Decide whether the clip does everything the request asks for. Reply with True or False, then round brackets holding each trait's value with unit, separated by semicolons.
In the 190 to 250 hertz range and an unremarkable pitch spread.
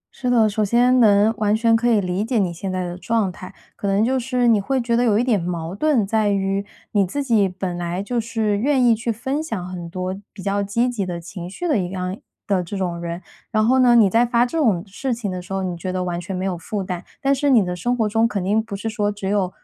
True (205 Hz; 4.1 semitones)